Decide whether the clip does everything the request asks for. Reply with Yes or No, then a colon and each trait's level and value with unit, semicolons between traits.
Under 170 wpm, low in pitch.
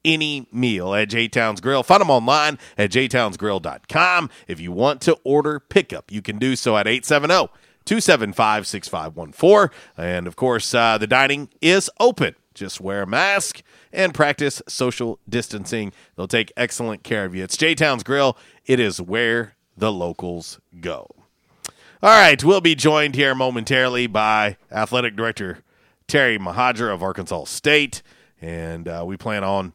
Yes: average, 155 wpm; low, 120 Hz